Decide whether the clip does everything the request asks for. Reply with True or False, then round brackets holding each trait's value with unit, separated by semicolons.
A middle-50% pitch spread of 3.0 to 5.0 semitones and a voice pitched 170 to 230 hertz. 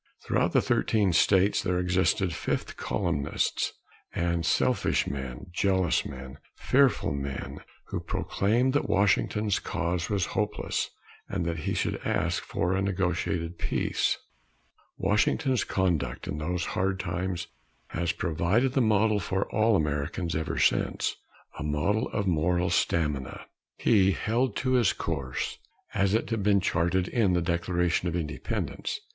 False (3.3 semitones; 90 Hz)